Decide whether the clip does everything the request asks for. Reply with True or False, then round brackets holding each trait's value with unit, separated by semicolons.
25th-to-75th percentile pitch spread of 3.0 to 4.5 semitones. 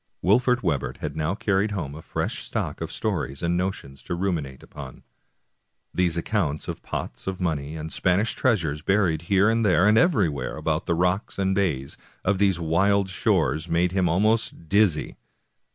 True (4.0 semitones)